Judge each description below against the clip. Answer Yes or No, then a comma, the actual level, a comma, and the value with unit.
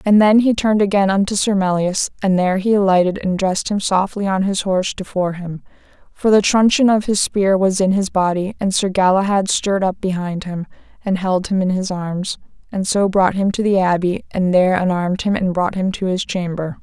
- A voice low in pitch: No, high, 190 Hz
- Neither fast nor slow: No, fast, 220 wpm